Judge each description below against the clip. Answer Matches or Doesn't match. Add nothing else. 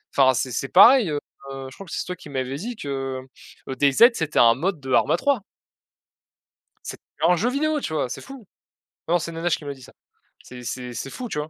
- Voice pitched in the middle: Matches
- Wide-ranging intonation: Matches